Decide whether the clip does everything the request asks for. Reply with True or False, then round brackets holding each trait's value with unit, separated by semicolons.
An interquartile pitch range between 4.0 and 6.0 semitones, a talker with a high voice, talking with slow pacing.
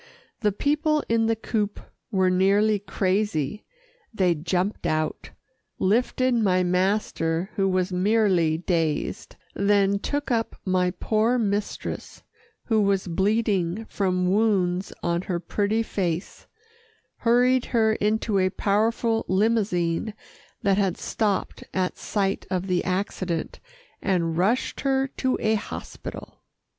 False (3.3 semitones; 200 Hz; 120 wpm)